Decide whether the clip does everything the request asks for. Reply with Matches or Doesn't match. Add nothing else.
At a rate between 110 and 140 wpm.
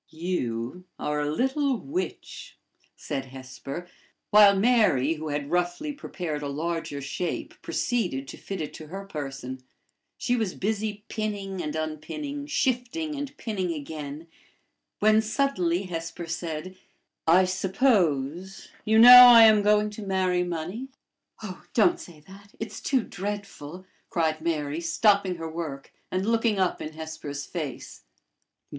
Matches